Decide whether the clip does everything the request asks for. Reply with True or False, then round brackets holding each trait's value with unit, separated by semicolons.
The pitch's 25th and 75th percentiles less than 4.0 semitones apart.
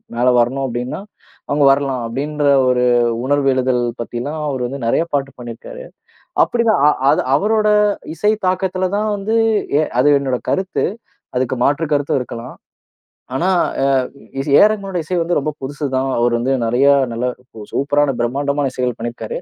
False (4.8 semitones)